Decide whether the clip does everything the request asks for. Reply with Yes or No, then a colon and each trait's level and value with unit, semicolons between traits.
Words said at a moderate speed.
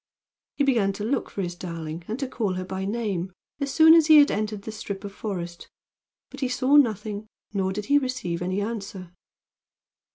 Yes: average, 195 wpm